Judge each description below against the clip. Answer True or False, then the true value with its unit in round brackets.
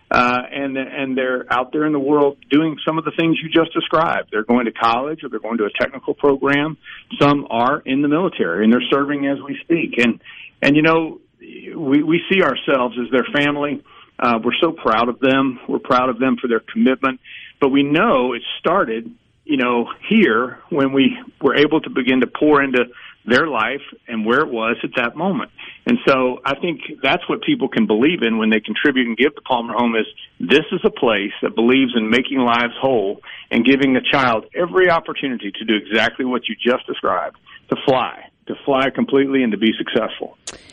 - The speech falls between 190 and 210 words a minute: True (205 wpm)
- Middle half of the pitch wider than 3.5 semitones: False (3.2 semitones)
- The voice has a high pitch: False (135 Hz)